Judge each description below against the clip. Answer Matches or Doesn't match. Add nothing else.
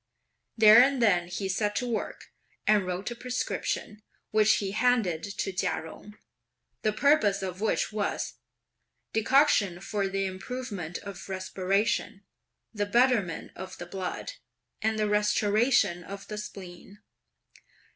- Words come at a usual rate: Doesn't match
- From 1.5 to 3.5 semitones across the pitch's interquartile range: Matches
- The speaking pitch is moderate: Doesn't match